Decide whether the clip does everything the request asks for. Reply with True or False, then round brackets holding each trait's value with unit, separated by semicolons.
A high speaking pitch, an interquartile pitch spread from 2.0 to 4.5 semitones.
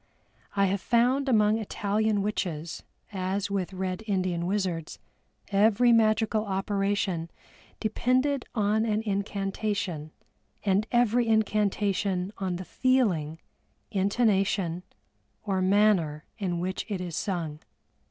True (200 Hz; 2.7 semitones)